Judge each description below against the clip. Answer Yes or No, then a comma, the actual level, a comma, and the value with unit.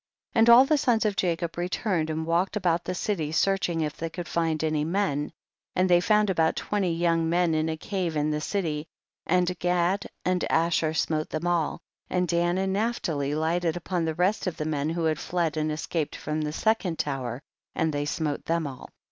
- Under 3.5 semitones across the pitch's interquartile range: Yes, average, 2.7 semitones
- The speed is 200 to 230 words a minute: Yes, fast, 205 wpm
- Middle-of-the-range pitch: Yes, medium, 170 Hz